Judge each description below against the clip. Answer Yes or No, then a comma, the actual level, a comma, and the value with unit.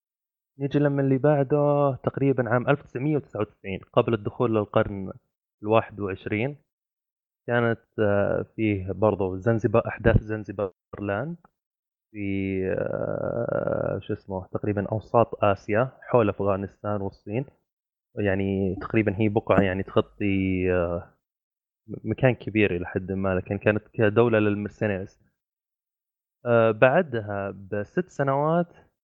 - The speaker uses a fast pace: No, average, 95 wpm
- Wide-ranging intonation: No, average, 3.9 semitones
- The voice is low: Yes, low, 105 Hz